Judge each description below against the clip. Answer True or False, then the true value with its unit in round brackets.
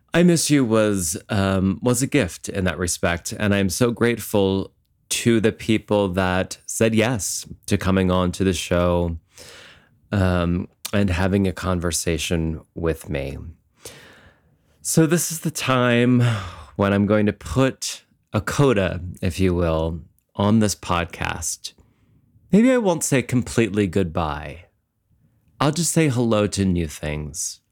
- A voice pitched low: True (100 Hz)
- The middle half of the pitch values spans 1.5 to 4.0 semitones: False (5.1 semitones)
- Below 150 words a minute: True (140 wpm)